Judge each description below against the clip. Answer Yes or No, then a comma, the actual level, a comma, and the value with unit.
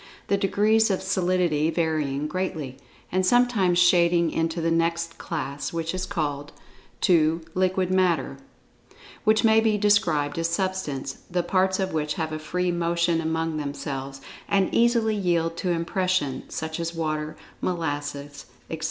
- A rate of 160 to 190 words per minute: No, average, 145 wpm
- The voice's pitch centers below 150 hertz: No, medium, 170 Hz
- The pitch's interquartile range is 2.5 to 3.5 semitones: Yes, average, 3.2 semitones